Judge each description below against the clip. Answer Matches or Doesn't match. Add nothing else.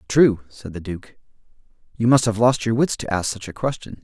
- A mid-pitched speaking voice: Doesn't match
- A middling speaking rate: Doesn't match